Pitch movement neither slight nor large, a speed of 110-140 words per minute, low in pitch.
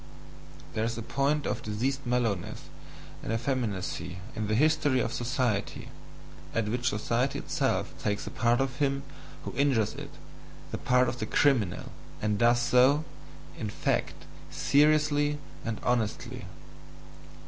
Yes: average, 4.0 semitones; slow, 135 wpm; low, 120 Hz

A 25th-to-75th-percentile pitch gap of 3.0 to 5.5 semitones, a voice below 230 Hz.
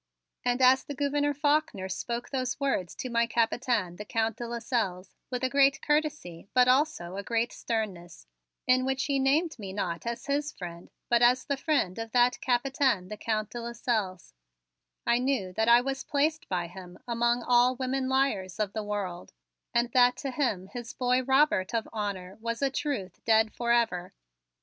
No: average, 4.3 semitones; high, 240 Hz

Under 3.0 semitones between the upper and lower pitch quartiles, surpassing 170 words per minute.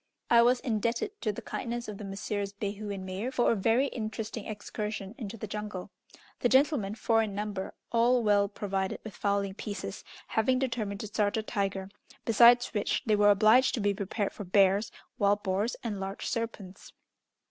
Yes: narrow, 2.4 semitones; average, 180 wpm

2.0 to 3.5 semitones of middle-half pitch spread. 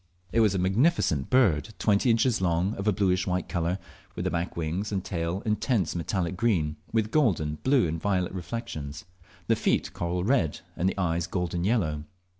No: average, 4.4 semitones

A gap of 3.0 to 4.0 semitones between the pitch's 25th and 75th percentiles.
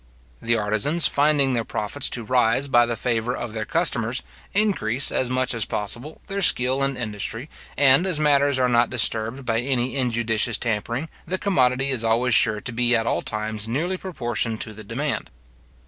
Yes: average, 3.5 semitones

